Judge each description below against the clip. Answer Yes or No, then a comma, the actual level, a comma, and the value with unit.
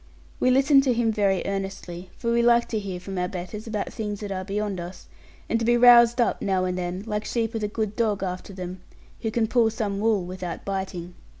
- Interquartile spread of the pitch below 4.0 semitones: Yes, average, 3.6 semitones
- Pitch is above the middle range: Yes, high, 205 Hz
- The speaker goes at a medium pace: No, fast, 225 wpm